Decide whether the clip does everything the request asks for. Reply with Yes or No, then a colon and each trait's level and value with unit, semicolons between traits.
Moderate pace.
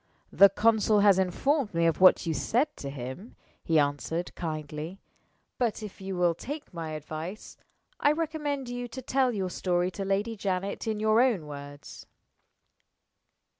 Yes: average, 155 wpm